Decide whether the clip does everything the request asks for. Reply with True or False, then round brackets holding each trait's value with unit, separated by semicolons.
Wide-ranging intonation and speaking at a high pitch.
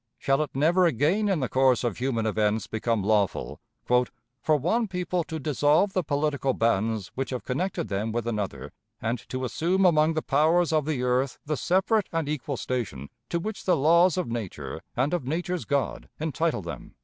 False (6.1 semitones; 140 Hz)